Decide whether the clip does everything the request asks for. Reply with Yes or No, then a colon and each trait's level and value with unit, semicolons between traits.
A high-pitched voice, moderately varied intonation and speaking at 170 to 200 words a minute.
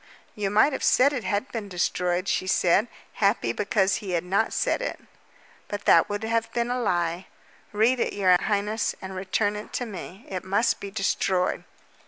Yes: high, 205 Hz; average, 3.1 semitones; average, 185 wpm